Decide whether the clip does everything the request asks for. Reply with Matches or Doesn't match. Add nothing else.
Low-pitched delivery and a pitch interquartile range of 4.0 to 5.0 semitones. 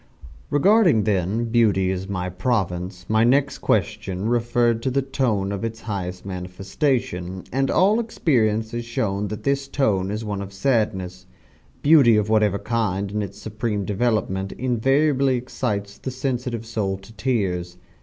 Matches